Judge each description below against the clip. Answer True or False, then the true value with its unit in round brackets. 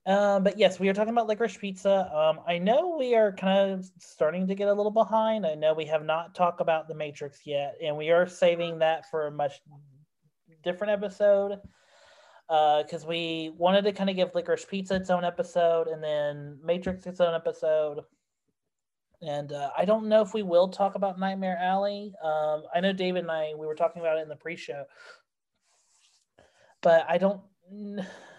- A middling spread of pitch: True (3.8 semitones)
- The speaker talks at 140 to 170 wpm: False (190 wpm)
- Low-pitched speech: False (175 Hz)